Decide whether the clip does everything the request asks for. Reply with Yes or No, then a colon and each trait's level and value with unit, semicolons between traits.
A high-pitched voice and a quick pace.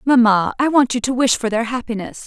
Yes: high, 240 Hz; fast, 240 wpm